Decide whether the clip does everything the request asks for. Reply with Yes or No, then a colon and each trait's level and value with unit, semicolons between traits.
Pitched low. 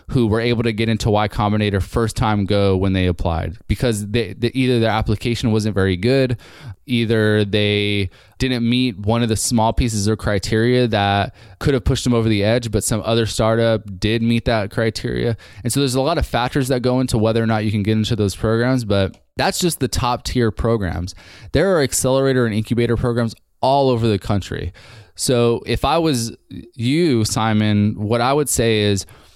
Yes: low, 115 Hz